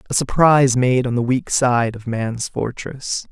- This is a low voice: Yes, low, 125 Hz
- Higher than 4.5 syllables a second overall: No, 4.2 syllables/s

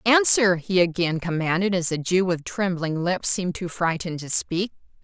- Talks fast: No, average, 180 wpm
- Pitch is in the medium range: Yes, medium, 180 Hz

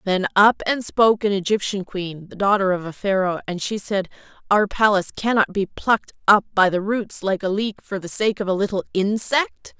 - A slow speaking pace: No, average, 195 wpm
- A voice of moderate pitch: No, high, 200 Hz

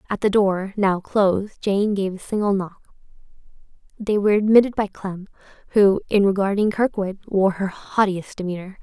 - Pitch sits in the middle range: No, high, 200 Hz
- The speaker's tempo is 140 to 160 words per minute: Yes, average, 155 wpm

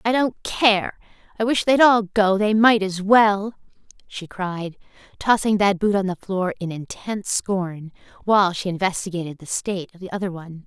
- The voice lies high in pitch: Yes, high, 195 Hz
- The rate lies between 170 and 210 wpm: Yes, average, 180 wpm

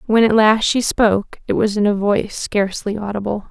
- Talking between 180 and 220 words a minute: Yes, fast, 205 wpm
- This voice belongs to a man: No, female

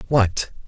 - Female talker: Yes, female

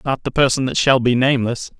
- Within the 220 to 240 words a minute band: Yes, fast, 235 wpm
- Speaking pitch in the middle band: No, low, 130 Hz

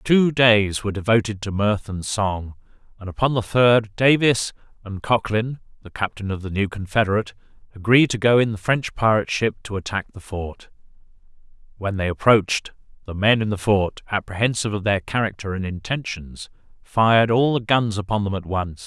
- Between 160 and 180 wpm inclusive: Yes, average, 175 wpm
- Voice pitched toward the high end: No, low, 105 Hz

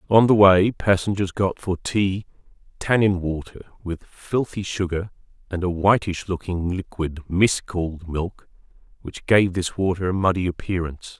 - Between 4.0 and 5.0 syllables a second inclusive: Yes, 4.5 syllables/s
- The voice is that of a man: Yes, male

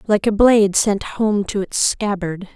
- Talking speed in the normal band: Yes, average, 190 wpm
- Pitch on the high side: Yes, high, 205 Hz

